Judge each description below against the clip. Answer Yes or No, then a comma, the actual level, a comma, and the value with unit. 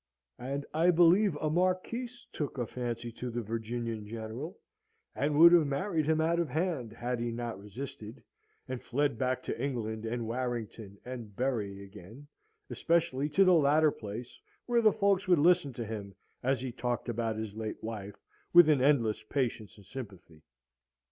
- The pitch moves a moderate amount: No, wide, 5.8 semitones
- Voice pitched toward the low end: Yes, low, 125 Hz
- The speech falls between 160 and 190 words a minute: Yes, average, 170 wpm